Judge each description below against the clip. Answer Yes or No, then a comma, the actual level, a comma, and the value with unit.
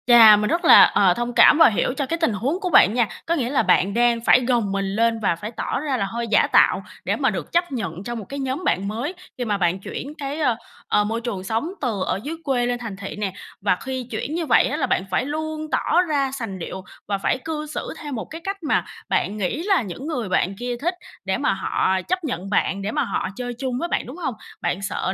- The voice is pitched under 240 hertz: No, high, 245 Hz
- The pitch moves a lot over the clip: Yes, wide, 6.1 semitones